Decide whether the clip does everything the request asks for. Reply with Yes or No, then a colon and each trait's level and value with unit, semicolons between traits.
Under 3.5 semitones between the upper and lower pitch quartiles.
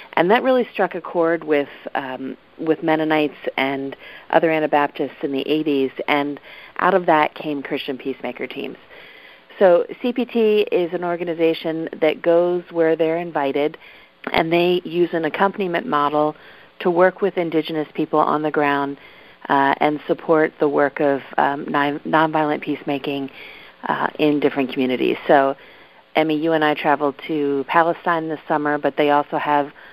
Yes: average, 2.7 semitones